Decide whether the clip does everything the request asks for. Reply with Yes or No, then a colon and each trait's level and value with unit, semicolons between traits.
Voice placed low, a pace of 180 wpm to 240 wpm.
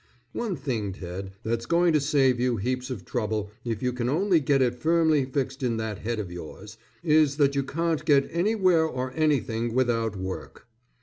Yes: low, 130 Hz; average, 185 wpm